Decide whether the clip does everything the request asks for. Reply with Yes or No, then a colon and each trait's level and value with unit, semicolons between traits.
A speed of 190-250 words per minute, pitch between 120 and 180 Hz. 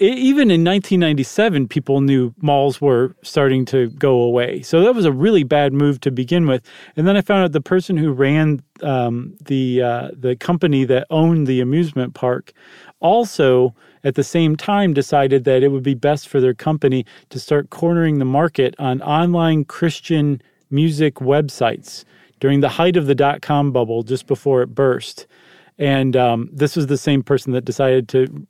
No: average, 180 wpm; medium, 140 Hz